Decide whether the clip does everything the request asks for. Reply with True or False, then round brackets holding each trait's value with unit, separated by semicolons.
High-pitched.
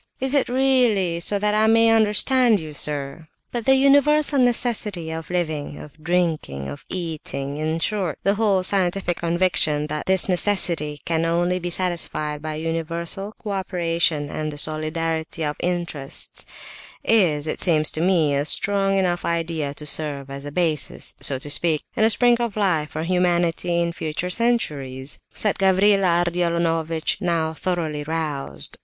False (170 Hz)